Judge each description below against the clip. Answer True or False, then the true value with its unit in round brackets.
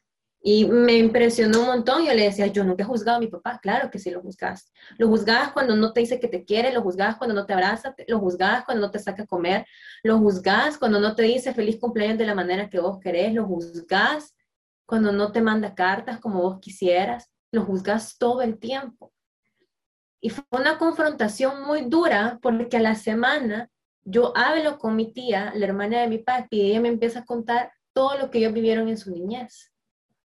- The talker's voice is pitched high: True (225 Hz)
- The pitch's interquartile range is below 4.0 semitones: True (3.1 semitones)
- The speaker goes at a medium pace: False (210 wpm)